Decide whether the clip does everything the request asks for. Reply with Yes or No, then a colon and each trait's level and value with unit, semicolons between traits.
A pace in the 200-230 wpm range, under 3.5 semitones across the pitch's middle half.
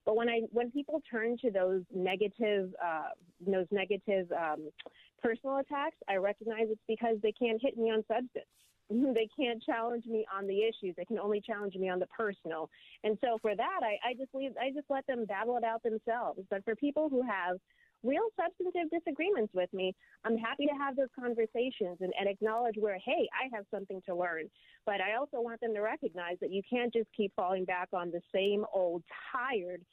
No: fast, 205 wpm; average, 3.9 semitones